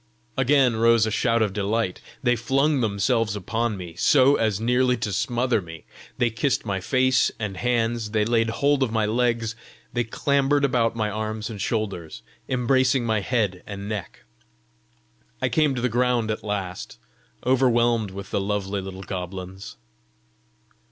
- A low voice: Yes, low, 115 Hz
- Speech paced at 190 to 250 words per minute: No, average, 155 wpm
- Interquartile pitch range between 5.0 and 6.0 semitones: No, average, 3.3 semitones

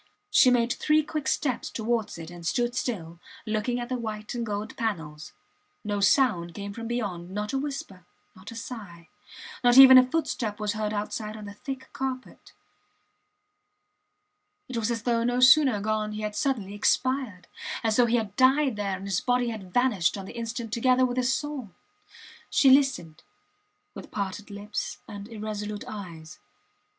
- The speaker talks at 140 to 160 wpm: No, average, 170 wpm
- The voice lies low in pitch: No, high, 220 Hz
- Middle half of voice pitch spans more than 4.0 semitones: No, average, 3.6 semitones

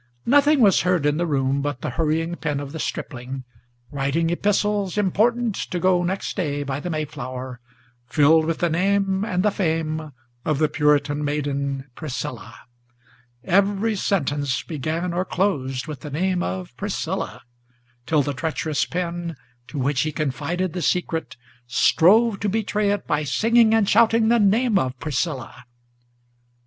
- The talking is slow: No, average, 150 wpm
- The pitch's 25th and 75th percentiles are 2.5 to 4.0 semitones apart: No, average, 5.2 semitones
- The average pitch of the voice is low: No, medium, 160 Hz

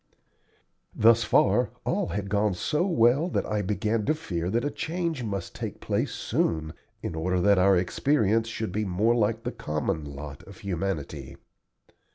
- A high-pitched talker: No, low, 105 Hz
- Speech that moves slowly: No, average, 165 wpm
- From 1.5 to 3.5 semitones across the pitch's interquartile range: No, average, 4.6 semitones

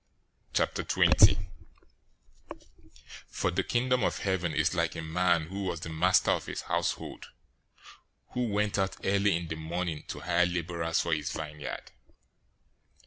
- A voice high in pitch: No, very low, 90 Hz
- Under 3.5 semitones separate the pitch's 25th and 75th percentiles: Yes, average, 3.1 semitones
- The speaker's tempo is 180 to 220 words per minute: No, average, 140 wpm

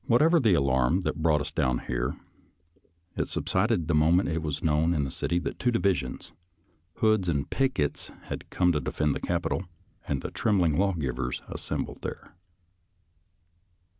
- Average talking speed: Yes, average, 155 wpm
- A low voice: Yes, very low, 80 Hz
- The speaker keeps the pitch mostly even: No, average, 4.3 semitones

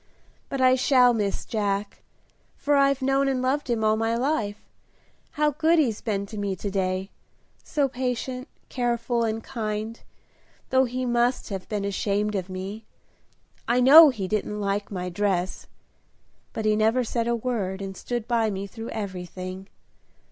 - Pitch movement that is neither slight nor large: Yes, average, 4.0 semitones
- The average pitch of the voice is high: Yes, high, 225 Hz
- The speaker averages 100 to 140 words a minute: No, average, 160 wpm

